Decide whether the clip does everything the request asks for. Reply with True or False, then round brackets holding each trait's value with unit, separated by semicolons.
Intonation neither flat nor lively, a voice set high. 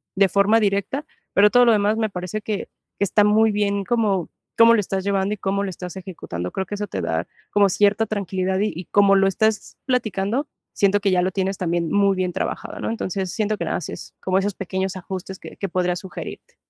False (2.0 semitones; 195 Hz)